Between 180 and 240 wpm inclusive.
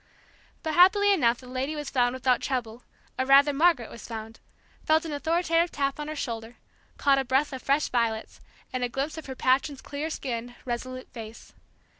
Yes: average, 185 wpm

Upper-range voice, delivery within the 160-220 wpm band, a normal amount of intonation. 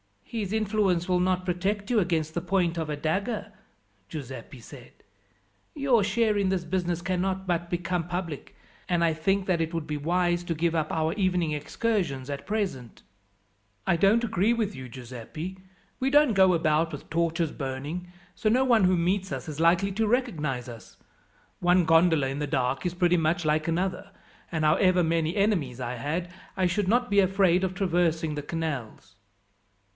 No: medium, 175 Hz; average, 175 wpm; average, 3.6 semitones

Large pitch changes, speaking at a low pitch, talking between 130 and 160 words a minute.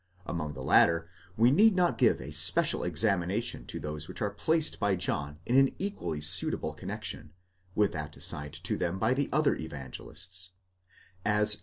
No: wide, 7.3 semitones; very low, 95 Hz; average, 170 wpm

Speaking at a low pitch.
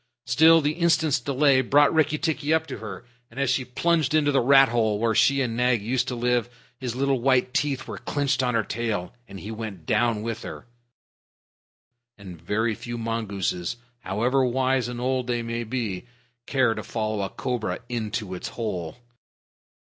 Yes: low, 120 Hz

